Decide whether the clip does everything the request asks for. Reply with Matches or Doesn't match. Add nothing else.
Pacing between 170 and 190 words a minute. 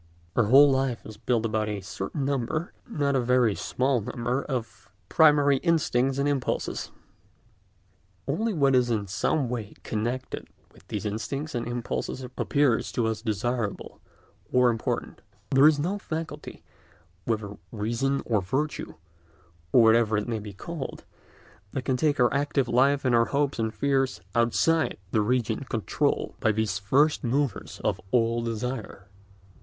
Doesn't match